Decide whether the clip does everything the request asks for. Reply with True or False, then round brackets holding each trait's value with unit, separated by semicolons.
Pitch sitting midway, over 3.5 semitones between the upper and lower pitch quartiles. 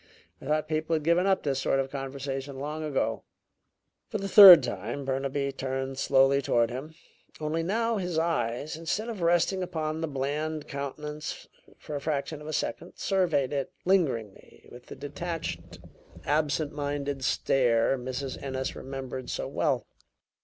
False (145 Hz; 3.2 semitones)